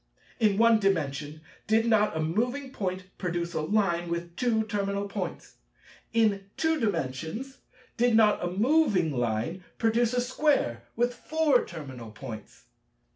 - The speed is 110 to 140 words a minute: Yes, slow, 135 wpm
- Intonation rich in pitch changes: Yes, wide, 6.0 semitones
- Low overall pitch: No, high, 200 Hz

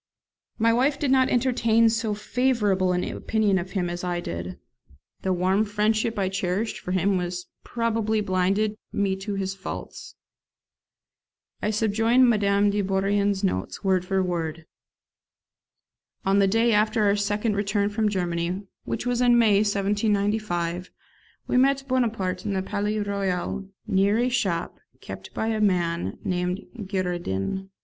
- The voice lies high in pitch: Yes, high, 200 Hz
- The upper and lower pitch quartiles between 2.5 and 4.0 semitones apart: Yes, average, 2.8 semitones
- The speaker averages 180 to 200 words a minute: No, average, 140 wpm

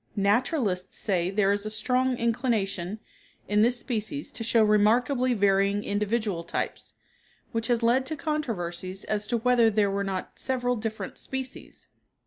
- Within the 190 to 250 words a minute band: No, average, 145 wpm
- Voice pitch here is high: Yes, high, 220 Hz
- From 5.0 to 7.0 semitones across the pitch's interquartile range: No, average, 3.6 semitones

